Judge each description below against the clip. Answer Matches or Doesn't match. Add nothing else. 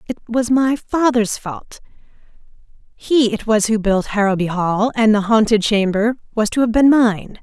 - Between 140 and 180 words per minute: Matches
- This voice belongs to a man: Doesn't match